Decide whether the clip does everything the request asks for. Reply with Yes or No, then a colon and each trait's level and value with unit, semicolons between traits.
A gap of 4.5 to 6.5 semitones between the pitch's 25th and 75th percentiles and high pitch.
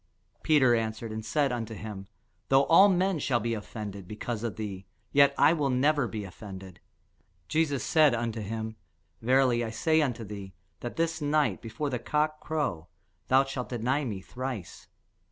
No: average, 4.9 semitones; low, 120 Hz